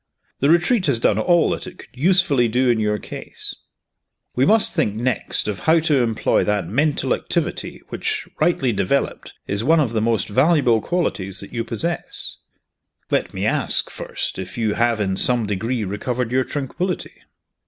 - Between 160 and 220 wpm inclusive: Yes, average, 170 wpm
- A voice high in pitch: No, low, 120 Hz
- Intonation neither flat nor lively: No, wide, 6.4 semitones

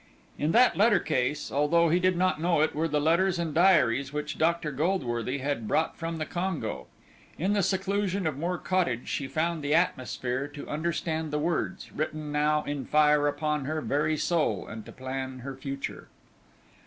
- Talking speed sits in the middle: Yes, average, 180 wpm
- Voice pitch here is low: No, medium, 155 Hz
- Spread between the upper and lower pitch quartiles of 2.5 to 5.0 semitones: Yes, average, 3.2 semitones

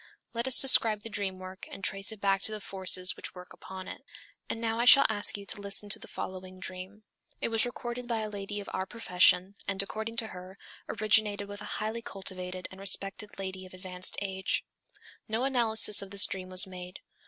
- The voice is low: No, high, 200 Hz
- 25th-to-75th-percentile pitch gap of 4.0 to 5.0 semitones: No, average, 2.7 semitones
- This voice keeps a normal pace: No, fast, 210 wpm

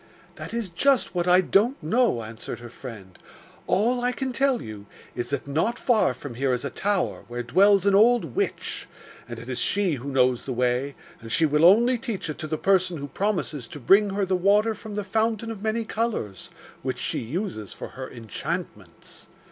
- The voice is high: No, medium, 180 Hz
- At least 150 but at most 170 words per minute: No, average, 200 wpm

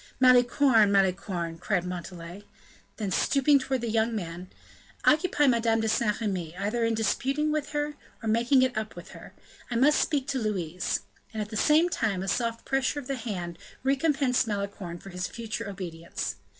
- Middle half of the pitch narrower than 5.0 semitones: No, wide, 5.5 semitones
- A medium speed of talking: Yes, average, 175 wpm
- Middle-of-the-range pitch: No, high, 225 Hz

